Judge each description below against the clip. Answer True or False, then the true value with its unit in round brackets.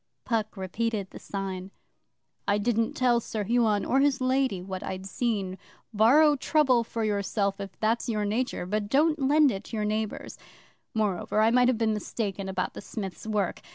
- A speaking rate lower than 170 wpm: False (175 wpm)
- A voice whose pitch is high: True (215 Hz)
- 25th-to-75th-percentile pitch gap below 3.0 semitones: False (3.5 semitones)